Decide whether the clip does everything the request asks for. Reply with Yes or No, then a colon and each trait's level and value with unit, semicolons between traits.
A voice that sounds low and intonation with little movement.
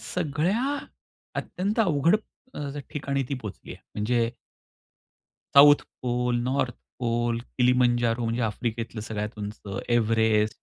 No: low, 120 Hz; average, 3.6 semitones